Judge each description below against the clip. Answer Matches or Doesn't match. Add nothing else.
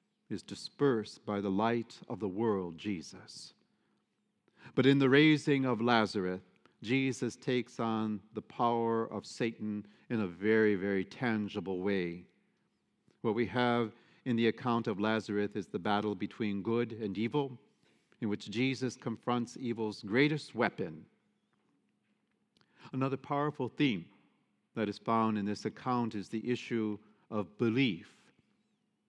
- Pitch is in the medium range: Doesn't match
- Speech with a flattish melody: Doesn't match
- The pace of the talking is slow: Matches